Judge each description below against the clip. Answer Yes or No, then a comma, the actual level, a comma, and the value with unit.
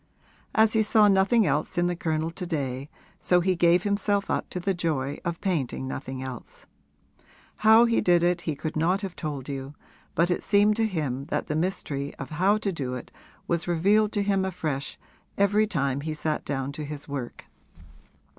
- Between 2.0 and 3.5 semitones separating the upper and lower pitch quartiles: No, wide, 5.6 semitones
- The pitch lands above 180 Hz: No, medium, 170 Hz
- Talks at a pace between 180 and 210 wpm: Yes, average, 190 wpm